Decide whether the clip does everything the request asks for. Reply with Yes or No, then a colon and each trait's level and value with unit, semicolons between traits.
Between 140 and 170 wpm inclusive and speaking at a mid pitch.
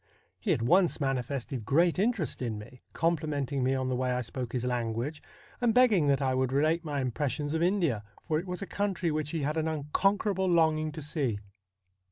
No: average, 200 wpm; medium, 150 Hz